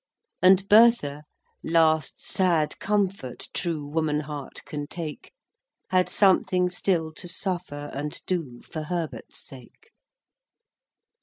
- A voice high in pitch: No, medium, 165 Hz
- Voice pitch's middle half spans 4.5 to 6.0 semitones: No, average, 3.7 semitones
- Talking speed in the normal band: No, slow, 100 wpm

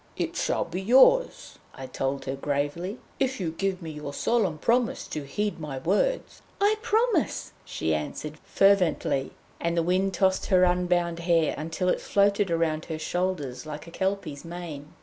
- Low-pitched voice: No, medium, 175 Hz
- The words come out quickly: No, average, 165 wpm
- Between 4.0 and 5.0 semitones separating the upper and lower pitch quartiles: Yes, average, 4.4 semitones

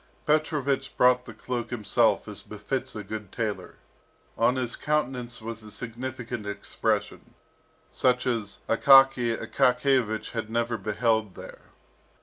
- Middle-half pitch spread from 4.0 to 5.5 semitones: No, average, 2.9 semitones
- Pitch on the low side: Yes, low, 120 Hz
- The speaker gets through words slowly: Yes, slow, 125 wpm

